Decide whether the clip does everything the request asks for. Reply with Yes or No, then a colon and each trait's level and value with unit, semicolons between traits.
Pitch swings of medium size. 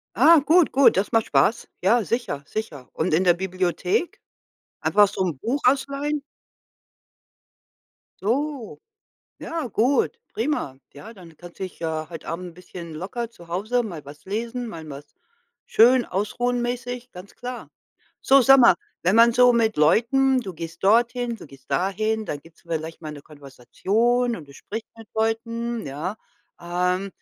No: wide, 6.2 semitones